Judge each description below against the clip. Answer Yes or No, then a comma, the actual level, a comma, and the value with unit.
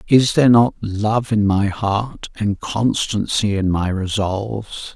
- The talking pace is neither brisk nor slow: Yes, average, 145 wpm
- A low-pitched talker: Yes, low, 105 Hz